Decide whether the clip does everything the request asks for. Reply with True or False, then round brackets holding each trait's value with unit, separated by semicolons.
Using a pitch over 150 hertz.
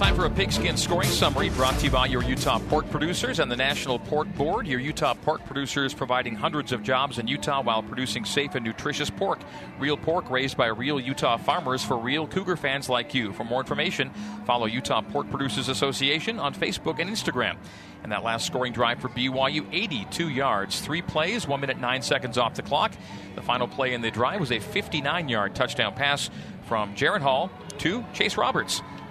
False (130 Hz)